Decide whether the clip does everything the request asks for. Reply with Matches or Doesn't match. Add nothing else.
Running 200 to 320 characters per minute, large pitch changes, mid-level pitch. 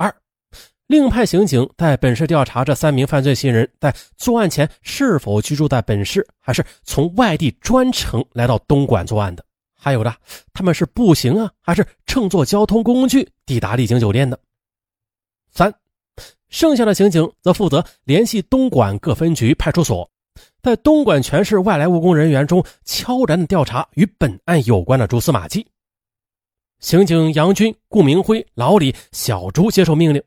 Matches